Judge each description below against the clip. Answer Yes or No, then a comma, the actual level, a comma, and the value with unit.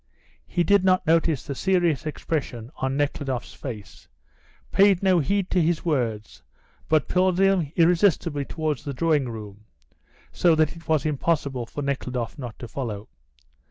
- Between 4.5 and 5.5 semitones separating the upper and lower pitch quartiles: Yes, average, 5.0 semitones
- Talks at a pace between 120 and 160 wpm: Yes, average, 150 wpm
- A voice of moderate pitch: Yes, medium, 150 Hz